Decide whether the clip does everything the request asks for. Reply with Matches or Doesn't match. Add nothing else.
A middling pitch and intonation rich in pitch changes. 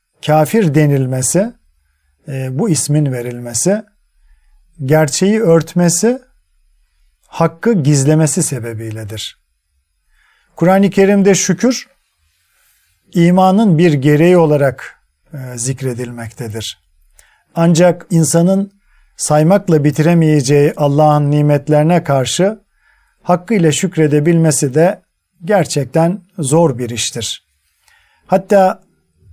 Matches